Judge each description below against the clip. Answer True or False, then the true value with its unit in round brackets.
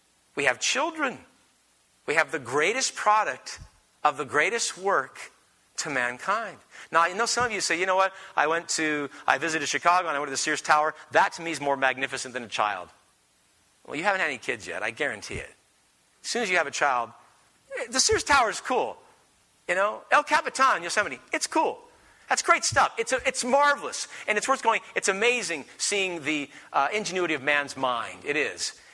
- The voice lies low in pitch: False (170 Hz)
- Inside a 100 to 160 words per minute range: False (200 wpm)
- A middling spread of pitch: False (9.0 semitones)